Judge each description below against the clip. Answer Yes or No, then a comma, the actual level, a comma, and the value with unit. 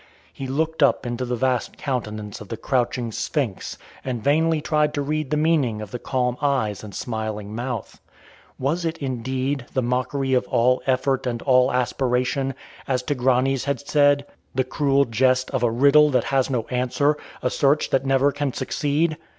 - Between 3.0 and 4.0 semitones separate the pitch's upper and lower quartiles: No, narrow, 2.5 semitones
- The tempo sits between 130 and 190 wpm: Yes, average, 175 wpm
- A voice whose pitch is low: Yes, low, 130 Hz